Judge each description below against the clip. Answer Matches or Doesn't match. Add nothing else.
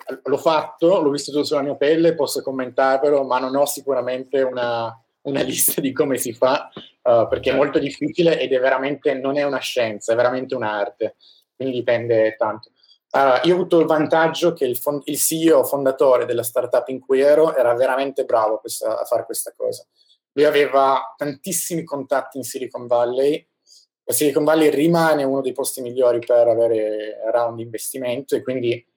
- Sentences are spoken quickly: Matches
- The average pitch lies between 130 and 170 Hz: Matches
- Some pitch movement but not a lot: Matches